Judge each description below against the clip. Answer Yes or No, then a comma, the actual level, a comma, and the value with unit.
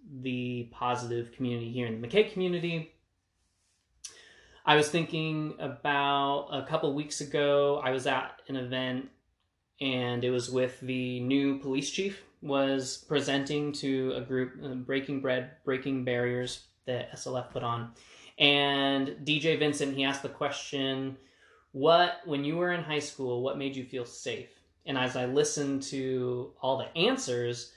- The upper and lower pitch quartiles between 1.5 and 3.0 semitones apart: Yes, narrow, 2.5 semitones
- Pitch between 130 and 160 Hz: Yes, low, 135 Hz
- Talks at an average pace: Yes, average, 155 wpm